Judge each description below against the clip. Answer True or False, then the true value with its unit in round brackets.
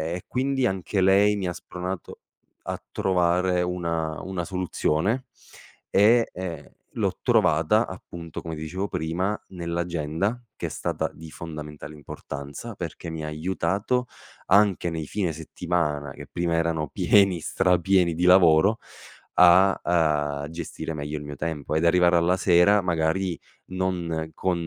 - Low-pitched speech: True (85 Hz)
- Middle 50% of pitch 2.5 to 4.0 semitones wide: True (2.8 semitones)